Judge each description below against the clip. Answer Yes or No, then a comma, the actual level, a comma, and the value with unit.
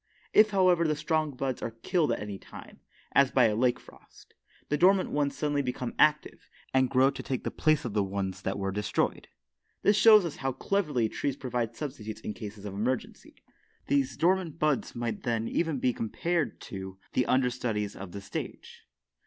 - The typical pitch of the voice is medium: No, low, 130 Hz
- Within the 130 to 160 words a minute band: No, average, 185 wpm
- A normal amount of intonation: No, wide, 5.7 semitones